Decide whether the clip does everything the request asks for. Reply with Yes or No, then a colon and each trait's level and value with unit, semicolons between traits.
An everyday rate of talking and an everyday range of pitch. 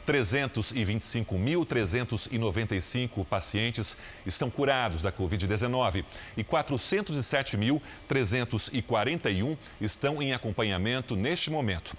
No: slow, 65 wpm; average, 4.8 semitones